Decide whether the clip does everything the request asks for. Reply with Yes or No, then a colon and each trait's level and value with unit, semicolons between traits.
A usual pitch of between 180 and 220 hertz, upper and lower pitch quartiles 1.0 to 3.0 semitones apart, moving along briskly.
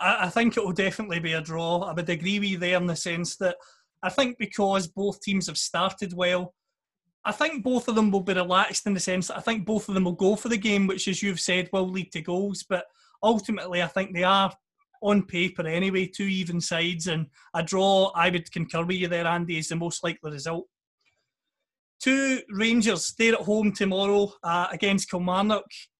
Yes: high, 190 Hz; narrow, 2.6 semitones; fast, 210 wpm